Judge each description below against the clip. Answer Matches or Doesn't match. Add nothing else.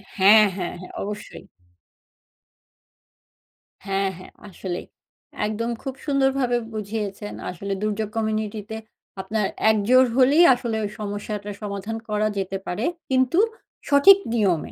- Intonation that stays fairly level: Doesn't match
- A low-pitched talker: Doesn't match